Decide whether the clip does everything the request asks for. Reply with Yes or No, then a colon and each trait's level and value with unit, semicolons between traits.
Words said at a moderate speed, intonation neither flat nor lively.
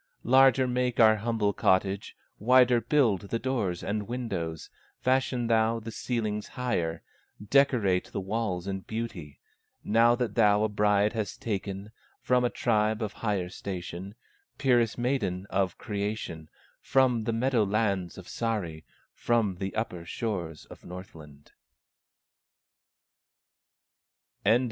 No: slow, 120 wpm; average, 3.7 semitones